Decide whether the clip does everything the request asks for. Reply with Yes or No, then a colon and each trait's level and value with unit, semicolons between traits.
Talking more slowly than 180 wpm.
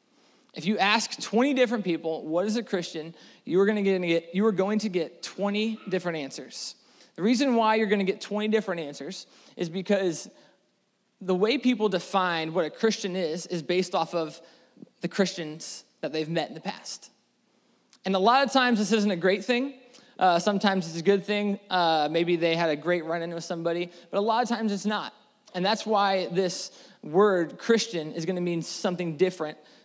No: average, 200 wpm